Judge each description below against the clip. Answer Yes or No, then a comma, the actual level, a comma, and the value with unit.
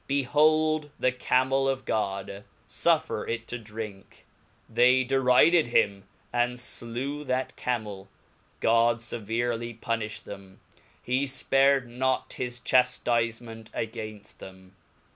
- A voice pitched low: Yes, low, 120 Hz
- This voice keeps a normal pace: No, slow, 110 wpm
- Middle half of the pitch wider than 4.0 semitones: No, average, 2.9 semitones